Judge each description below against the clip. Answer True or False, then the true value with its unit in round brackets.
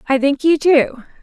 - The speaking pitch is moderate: False (300 Hz)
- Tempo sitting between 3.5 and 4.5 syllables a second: True (4.4 syllables/s)